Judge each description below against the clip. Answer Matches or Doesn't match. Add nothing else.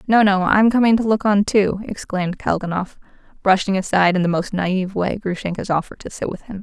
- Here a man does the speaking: Doesn't match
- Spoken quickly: Matches